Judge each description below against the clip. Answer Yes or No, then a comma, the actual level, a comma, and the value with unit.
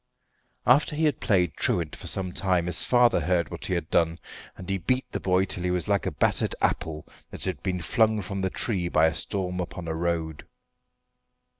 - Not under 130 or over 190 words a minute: No, fast, 205 wpm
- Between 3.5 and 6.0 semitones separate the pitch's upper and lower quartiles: No, narrow, 2.6 semitones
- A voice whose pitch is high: No, very low, 90 Hz